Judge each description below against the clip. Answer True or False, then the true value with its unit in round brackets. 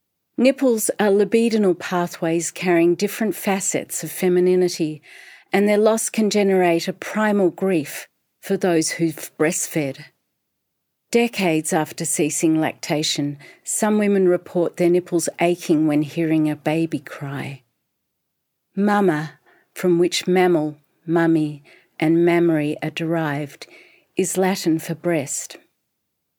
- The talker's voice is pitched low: False (170 Hz)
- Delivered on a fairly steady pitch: False (3.3 semitones)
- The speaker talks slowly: True (110 wpm)